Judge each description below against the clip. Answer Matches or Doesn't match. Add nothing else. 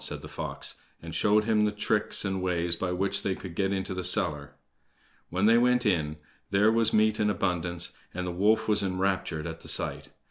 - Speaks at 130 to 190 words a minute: Doesn't match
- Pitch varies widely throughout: Doesn't match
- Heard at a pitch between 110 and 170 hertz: Doesn't match